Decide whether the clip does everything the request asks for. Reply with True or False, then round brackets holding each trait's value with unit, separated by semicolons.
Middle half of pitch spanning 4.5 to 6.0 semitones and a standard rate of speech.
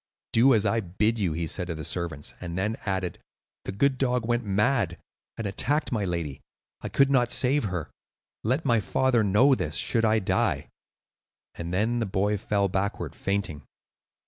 True (4.8 semitones; 175 wpm)